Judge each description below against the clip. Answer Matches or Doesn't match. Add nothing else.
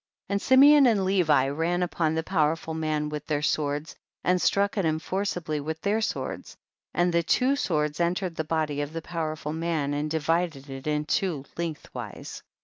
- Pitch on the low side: Doesn't match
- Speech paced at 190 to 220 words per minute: Matches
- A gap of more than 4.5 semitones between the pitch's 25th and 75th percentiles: Doesn't match